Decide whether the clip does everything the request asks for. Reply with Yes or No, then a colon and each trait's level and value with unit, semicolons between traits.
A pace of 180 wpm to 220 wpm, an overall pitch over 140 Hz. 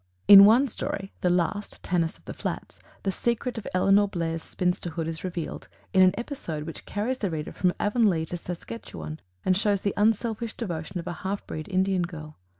Yes: average, 185 wpm; medium, 185 Hz